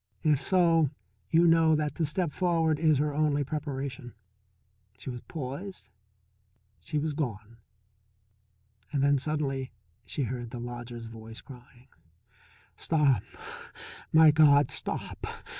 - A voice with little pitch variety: No, average, 3.8 semitones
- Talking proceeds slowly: Yes, slow, 115 wpm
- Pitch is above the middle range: No, medium, 145 Hz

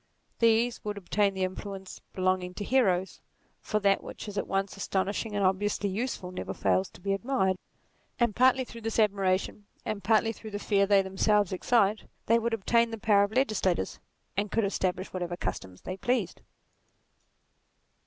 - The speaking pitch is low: No, high, 200 Hz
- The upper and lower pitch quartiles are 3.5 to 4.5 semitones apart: No, average, 2.9 semitones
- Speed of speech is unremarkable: Yes, average, 165 wpm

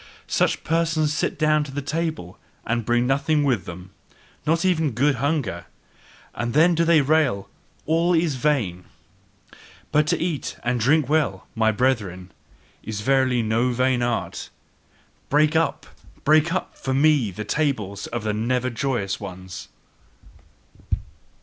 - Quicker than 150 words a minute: No, average, 140 wpm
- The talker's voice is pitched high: No, low, 135 Hz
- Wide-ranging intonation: Yes, wide, 5.8 semitones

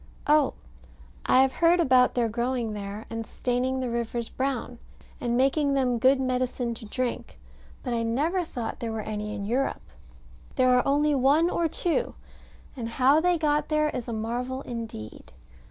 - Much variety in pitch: No, average, 3.1 semitones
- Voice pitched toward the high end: Yes, very high, 255 Hz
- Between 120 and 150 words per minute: No, average, 170 wpm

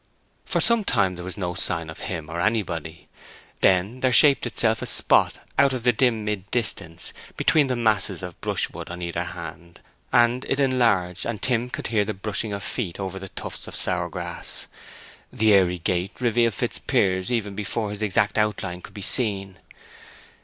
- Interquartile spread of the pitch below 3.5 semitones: No, average, 4.5 semitones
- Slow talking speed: No, average, 180 wpm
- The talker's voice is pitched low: Yes, low, 100 Hz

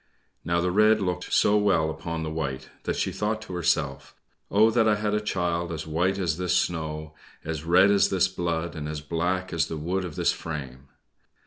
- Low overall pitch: Yes, very low, 85 Hz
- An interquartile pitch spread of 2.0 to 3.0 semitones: No, average, 3.4 semitones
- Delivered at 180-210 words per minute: Yes, fast, 205 wpm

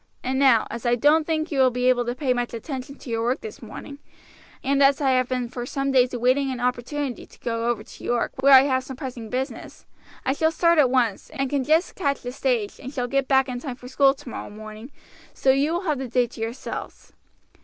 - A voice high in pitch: Yes, very high, 260 Hz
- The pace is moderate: No, fast, 240 wpm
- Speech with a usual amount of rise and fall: No, narrow, 2.2 semitones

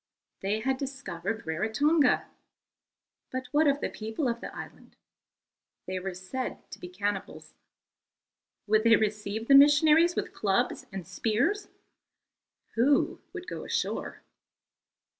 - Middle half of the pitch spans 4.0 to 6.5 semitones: Yes, wide, 5.6 semitones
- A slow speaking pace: Yes, slow, 120 wpm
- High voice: Yes, high, 225 Hz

